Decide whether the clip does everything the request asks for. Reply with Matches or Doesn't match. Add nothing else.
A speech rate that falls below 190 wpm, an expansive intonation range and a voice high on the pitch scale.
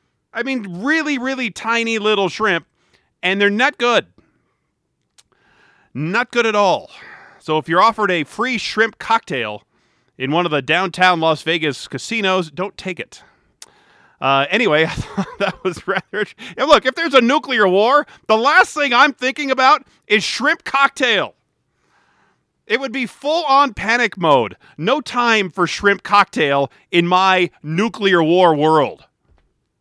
Matches